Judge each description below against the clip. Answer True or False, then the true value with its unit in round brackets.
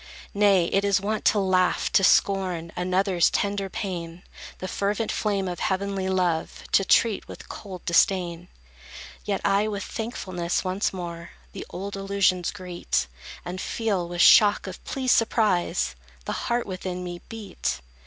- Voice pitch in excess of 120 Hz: True (190 Hz)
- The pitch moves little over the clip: True (2.1 semitones)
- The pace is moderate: True (145 wpm)